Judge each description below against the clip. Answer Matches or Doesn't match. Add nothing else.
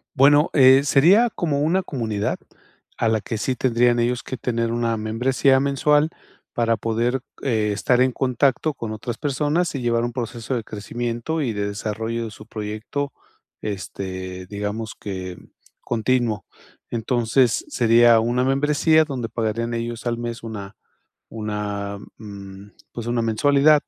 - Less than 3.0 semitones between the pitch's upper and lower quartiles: Doesn't match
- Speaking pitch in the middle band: Doesn't match